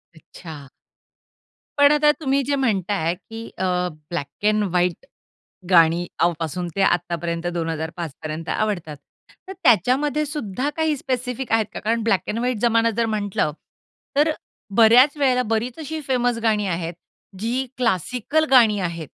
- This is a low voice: No, high, 220 Hz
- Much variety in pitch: Yes, wide, 6.6 semitones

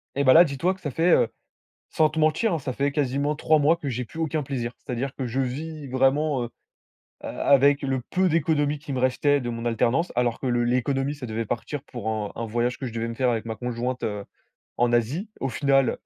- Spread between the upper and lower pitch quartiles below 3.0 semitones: No, average, 3.6 semitones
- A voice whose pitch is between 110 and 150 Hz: Yes, low, 135 Hz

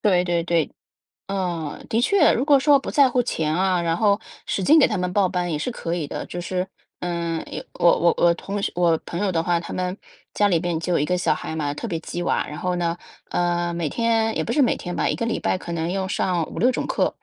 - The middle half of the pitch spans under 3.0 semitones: No, average, 3.3 semitones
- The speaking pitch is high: No, medium, 180 Hz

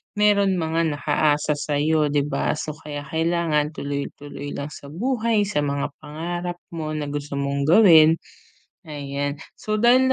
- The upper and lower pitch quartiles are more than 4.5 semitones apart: No, average, 3.3 semitones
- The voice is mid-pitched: Yes, medium, 155 Hz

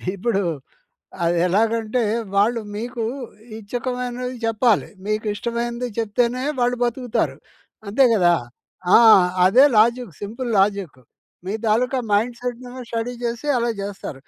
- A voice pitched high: Yes, high, 235 Hz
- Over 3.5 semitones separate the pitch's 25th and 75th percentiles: No, average, 3.1 semitones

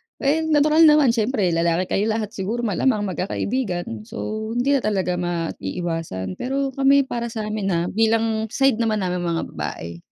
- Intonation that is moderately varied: No, wide, 6.1 semitones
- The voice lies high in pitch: Yes, high, 215 Hz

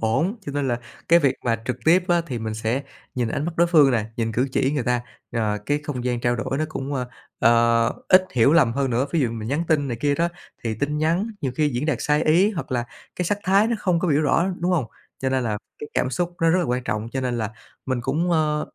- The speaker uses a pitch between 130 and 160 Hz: Yes, low, 135 Hz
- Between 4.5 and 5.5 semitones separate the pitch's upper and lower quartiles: Yes, average, 5.1 semitones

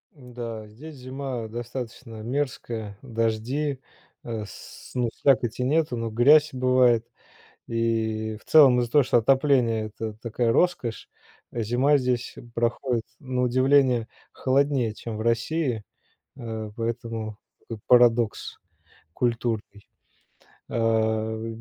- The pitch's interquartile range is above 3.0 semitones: No, narrow, 2.6 semitones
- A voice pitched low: Yes, low, 120 Hz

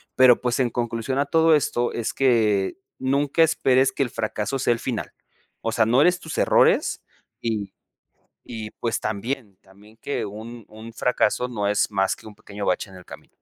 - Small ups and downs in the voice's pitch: No, average, 3.7 semitones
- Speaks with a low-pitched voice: Yes, low, 115 Hz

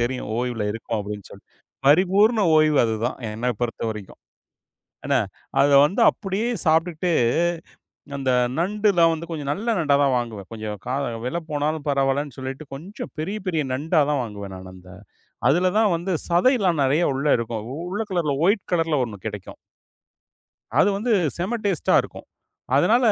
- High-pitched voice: No, medium, 150 Hz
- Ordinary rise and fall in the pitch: No, wide, 6.8 semitones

